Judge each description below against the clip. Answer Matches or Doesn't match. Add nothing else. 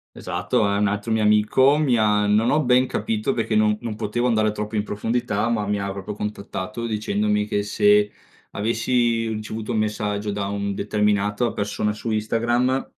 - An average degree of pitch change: Doesn't match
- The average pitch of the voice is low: Matches